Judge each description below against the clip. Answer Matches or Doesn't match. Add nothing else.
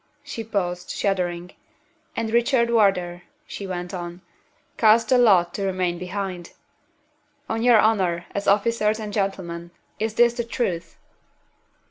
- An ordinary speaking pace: Doesn't match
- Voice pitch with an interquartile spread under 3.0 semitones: Doesn't match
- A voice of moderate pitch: Doesn't match